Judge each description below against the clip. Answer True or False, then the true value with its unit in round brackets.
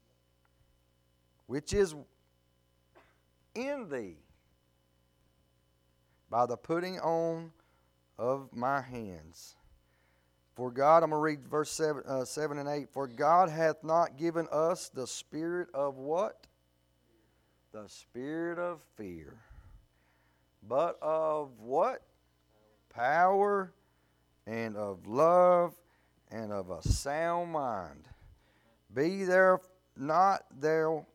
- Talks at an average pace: False (100 wpm)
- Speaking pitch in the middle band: False (115 Hz)